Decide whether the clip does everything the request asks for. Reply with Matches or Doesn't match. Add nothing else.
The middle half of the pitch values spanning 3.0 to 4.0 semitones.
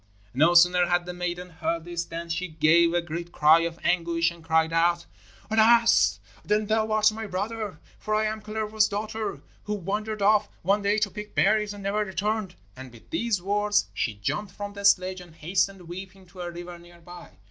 Matches